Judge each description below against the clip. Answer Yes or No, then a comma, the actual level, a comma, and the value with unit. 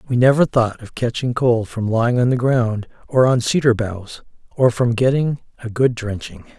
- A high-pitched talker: No, low, 120 Hz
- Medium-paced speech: Yes, average, 190 wpm